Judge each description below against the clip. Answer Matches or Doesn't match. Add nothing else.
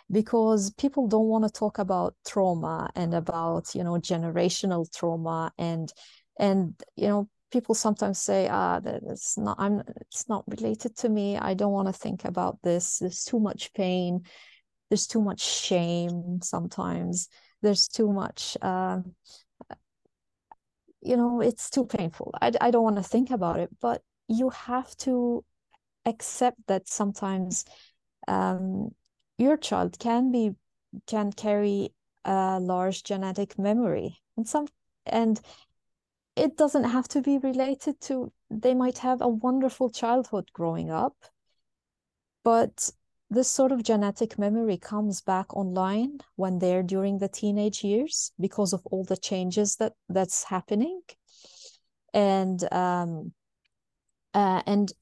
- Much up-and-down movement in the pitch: Doesn't match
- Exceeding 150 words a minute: Doesn't match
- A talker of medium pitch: Doesn't match